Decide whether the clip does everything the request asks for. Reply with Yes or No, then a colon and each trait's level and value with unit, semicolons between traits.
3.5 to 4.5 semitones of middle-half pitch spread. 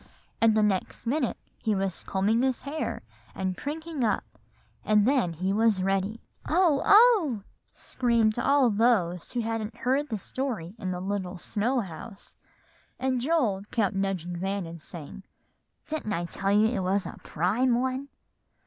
No: average, 5.1 semitones